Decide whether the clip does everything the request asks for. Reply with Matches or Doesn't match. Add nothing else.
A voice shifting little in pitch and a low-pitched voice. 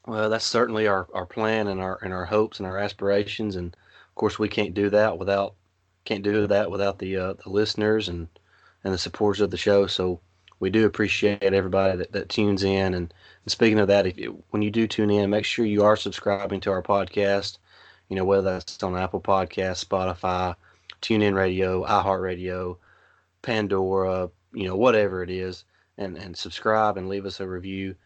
Matches